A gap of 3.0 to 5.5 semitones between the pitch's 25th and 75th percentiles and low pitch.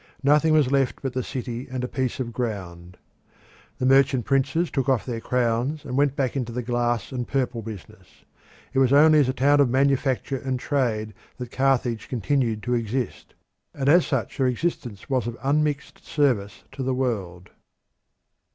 No: narrow, 2.6 semitones; low, 130 Hz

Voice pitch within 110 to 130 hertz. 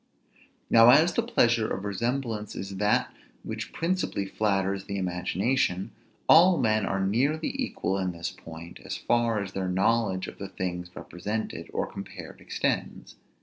No: low, 100 Hz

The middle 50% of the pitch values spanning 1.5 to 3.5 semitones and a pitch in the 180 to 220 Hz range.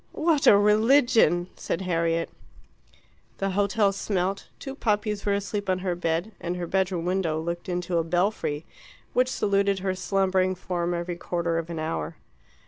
Yes: average, 2.7 semitones; medium, 185 Hz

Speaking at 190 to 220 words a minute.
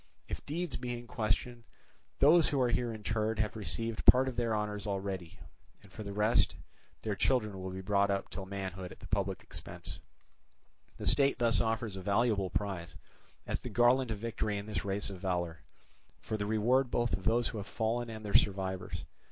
Yes: average, 195 wpm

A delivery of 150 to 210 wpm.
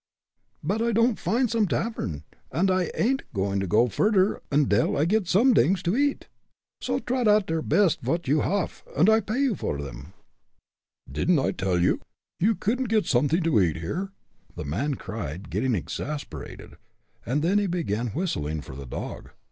Yes: average, 165 wpm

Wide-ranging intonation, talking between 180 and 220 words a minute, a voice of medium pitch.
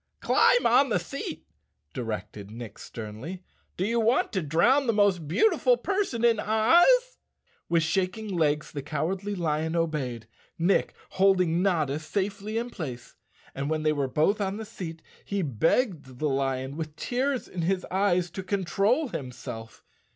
No: wide, 6.1 semitones; average, 160 wpm; medium, 180 Hz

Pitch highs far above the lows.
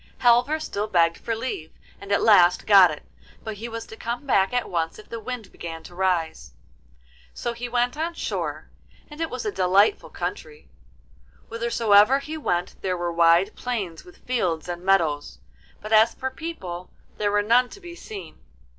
Yes: wide, 5.7 semitones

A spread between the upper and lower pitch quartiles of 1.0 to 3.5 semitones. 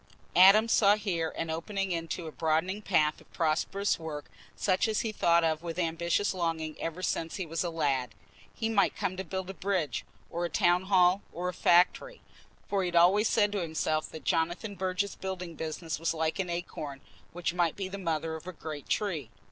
Yes: average, 3.0 semitones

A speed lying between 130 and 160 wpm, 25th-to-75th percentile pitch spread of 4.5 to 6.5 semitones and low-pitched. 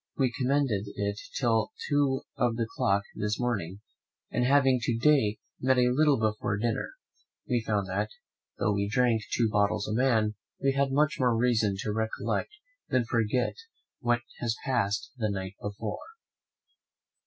No: average, 155 wpm; average, 3.6 semitones; low, 115 Hz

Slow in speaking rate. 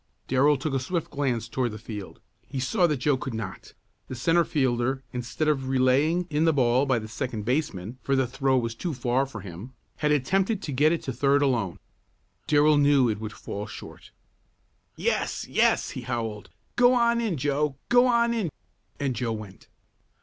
No: average, 185 wpm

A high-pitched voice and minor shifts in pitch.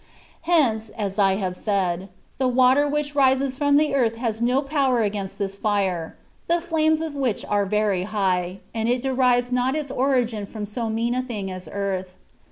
No: high, 230 Hz; average, 5.1 semitones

